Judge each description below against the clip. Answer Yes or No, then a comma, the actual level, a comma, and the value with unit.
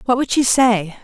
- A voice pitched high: Yes, high, 235 Hz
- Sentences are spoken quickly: Yes, fast, 230 wpm